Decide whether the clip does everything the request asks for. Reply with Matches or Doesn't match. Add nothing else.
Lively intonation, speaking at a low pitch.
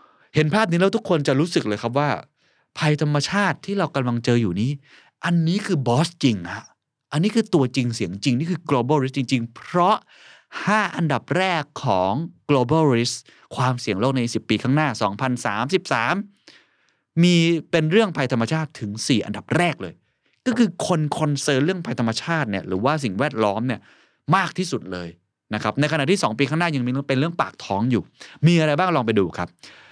Doesn't match